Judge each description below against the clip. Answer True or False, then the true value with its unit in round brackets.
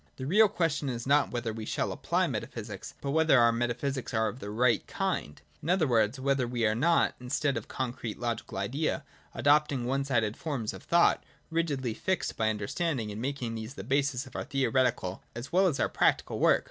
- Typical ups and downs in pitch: True (3.9 semitones)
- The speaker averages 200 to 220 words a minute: True (205 wpm)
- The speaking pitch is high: False (130 Hz)